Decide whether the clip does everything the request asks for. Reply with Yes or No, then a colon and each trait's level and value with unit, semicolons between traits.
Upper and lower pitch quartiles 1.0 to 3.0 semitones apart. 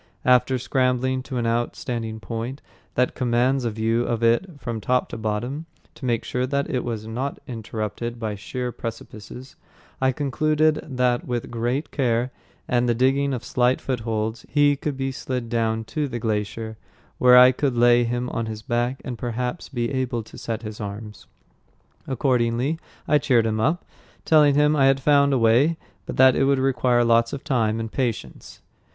Yes: narrow, 2.5 semitones